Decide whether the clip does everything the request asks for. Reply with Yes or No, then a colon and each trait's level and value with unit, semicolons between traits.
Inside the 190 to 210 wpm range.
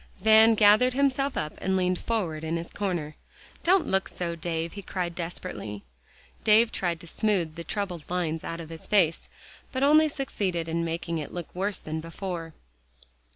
No: average, 170 wpm